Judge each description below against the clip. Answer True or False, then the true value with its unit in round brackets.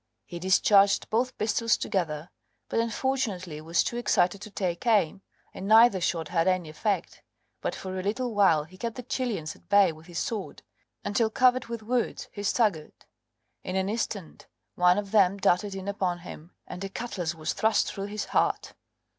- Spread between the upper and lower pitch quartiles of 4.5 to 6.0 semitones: False (3.9 semitones)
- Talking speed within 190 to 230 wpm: False (180 wpm)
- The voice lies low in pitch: False (195 Hz)